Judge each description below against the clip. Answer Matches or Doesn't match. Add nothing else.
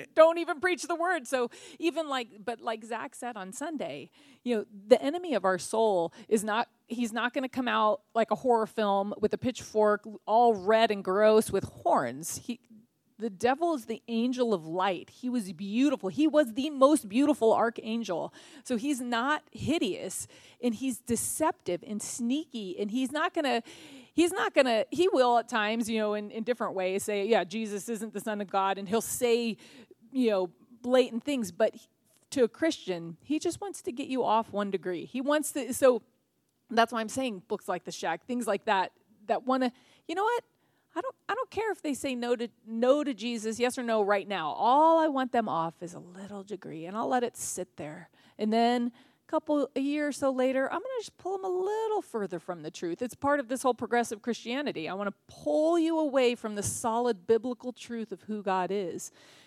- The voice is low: Doesn't match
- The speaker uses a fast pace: Matches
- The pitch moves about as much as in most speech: Matches